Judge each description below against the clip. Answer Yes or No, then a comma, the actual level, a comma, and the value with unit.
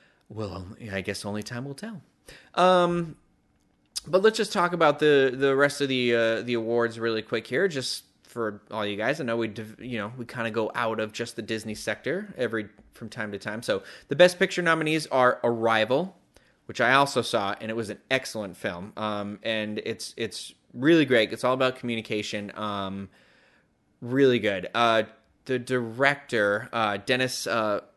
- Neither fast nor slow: Yes, average, 180 wpm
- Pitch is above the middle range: No, low, 115 Hz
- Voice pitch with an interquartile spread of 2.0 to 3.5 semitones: No, average, 4.0 semitones